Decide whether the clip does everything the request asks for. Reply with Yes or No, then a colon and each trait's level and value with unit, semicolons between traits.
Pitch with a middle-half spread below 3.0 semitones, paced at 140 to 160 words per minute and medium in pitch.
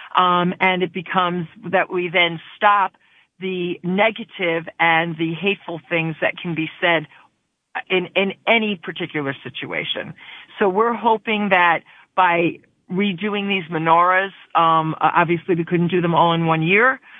Yes: narrow, 2.6 semitones; average, 145 wpm; medium, 180 Hz